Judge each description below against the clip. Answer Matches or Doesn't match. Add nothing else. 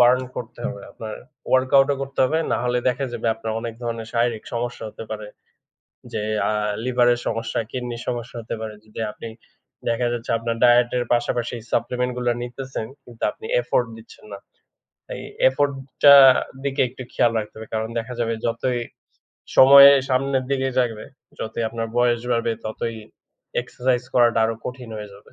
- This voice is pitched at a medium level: Doesn't match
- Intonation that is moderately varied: Doesn't match